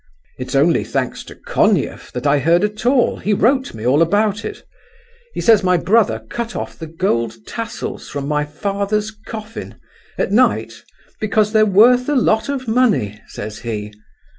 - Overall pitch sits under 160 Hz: No, high, 200 Hz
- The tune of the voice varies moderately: No, wide, 7.9 semitones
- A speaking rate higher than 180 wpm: No, average, 165 wpm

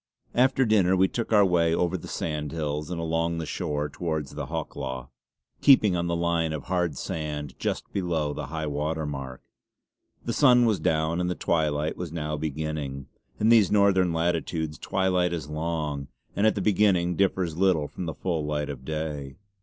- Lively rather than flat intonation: No, average, 3.3 semitones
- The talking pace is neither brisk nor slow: Yes, average, 175 wpm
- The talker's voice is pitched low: Yes, very low, 80 Hz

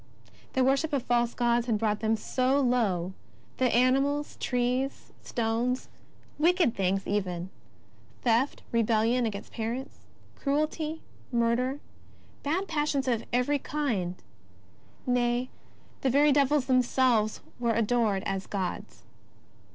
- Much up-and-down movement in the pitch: No, average, 3.4 semitones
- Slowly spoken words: Yes, slow, 120 wpm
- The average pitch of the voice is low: No, high, 245 Hz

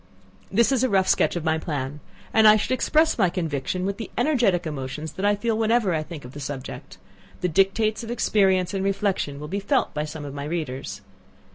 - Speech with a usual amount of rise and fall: No, wide, 6.2 semitones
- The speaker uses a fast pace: Yes, fast, 215 wpm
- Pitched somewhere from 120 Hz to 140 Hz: No, medium, 185 Hz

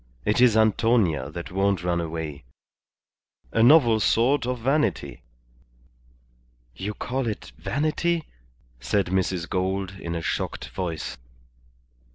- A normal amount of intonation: No, wide, 5.7 semitones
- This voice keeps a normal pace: No, slow, 115 wpm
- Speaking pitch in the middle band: No, low, 100 Hz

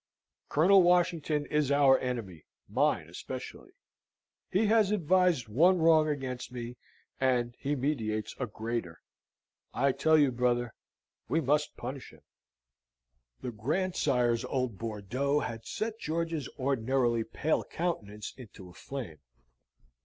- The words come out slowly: Yes, slow, 120 wpm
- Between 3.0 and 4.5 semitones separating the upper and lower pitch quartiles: No, average, 5.0 semitones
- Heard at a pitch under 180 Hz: Yes, low, 135 Hz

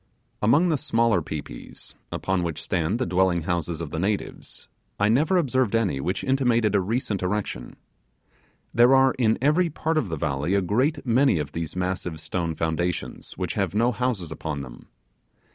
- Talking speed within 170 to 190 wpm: Yes, average, 175 wpm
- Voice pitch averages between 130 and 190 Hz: No, low, 100 Hz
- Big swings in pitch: Yes, wide, 6.9 semitones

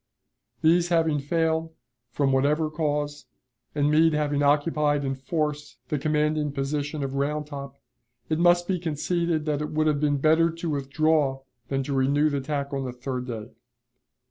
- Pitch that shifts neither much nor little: No, narrow, 2.1 semitones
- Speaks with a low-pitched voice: No, medium, 150 Hz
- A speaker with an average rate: Yes, average, 165 wpm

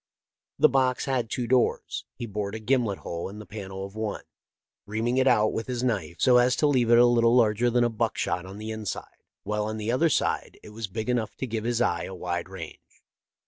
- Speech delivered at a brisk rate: Yes, fast, 225 wpm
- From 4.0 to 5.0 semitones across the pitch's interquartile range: No, average, 2.7 semitones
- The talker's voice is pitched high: No, low, 115 Hz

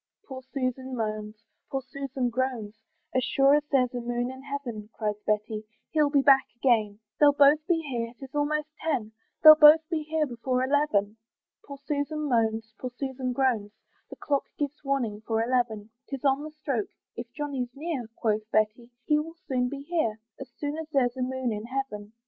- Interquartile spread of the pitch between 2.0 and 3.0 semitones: No, average, 3.9 semitones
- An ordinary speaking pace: Yes, average, 180 wpm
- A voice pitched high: Yes, very high, 260 Hz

